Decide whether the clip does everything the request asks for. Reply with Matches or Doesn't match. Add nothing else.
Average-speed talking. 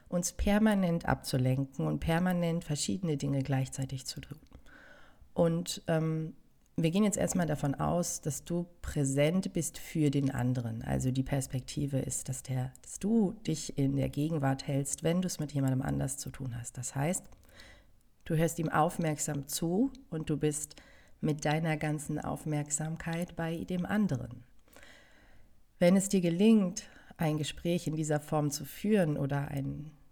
Matches